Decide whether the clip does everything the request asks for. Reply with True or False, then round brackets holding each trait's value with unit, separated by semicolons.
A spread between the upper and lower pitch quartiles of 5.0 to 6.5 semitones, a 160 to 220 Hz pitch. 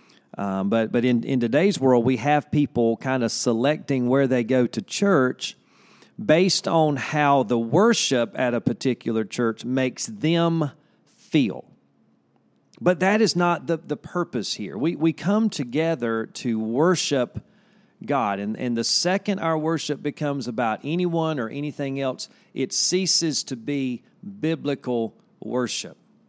False (5.3 semitones; 140 Hz)